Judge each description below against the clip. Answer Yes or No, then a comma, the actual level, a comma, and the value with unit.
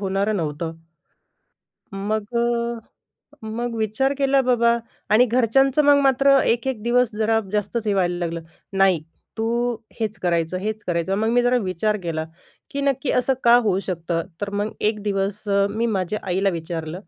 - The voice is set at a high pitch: Yes, high, 215 Hz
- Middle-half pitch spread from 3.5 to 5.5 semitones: Yes, average, 3.9 semitones